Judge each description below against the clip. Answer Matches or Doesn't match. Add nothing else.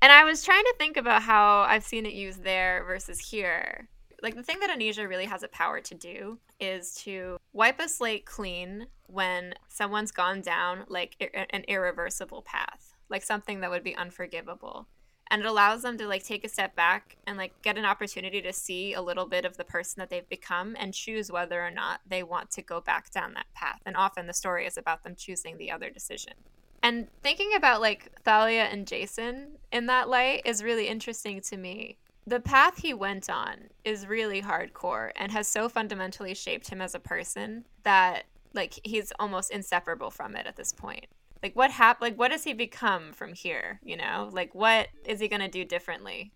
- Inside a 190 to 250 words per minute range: Matches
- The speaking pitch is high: Matches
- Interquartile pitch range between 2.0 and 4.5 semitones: Matches